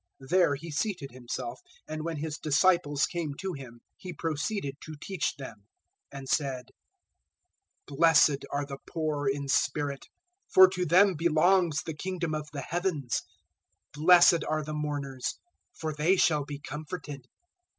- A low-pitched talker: No, medium, 150 Hz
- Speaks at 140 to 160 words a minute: Yes, average, 150 wpm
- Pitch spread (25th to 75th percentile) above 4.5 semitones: No, average, 3.4 semitones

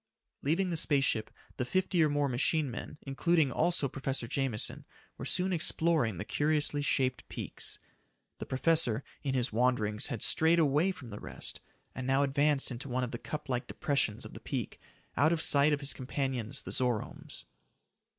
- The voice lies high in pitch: No, medium, 140 Hz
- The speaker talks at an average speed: Yes, average, 175 wpm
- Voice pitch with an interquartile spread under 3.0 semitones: No, average, 3.6 semitones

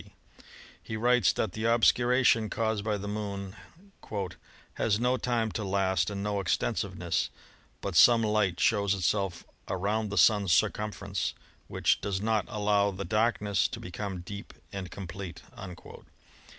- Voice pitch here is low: Yes, low, 105 Hz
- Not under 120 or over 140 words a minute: Yes, slow, 135 wpm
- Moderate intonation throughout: No, narrow, 2.0 semitones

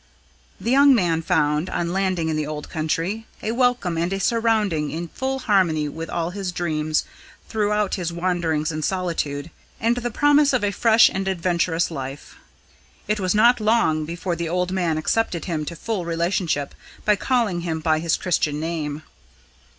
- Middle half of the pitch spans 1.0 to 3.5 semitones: No, average, 4.7 semitones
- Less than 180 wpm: Yes, average, 170 wpm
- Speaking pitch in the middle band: Yes, medium, 175 Hz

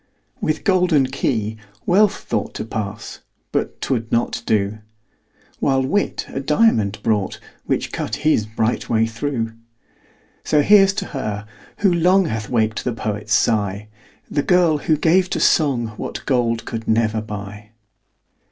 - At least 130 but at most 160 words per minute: Yes, average, 145 wpm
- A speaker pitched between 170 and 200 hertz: No, low, 115 Hz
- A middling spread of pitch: No, wide, 6.2 semitones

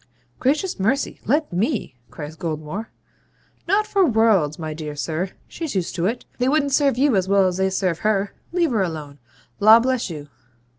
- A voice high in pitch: Yes, high, 200 Hz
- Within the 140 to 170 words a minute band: No, average, 180 wpm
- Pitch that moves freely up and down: Yes, wide, 8.1 semitones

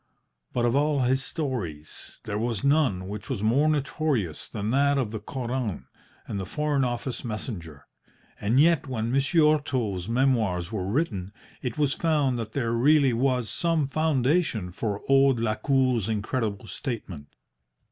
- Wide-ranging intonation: No, average, 4.8 semitones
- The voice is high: No, low, 125 Hz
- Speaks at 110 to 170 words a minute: Yes, average, 145 wpm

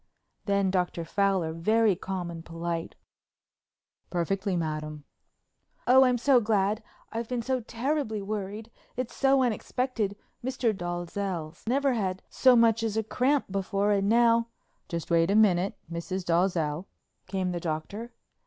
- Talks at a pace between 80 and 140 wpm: Yes, slow, 135 wpm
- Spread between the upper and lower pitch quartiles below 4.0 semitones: No, average, 4.8 semitones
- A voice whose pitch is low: No, high, 200 Hz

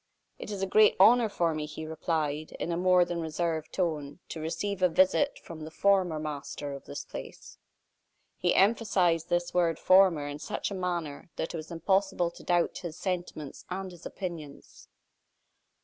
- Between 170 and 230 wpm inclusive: Yes, average, 175 wpm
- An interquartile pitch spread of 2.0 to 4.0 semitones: Yes, average, 3.1 semitones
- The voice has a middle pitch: Yes, medium, 175 Hz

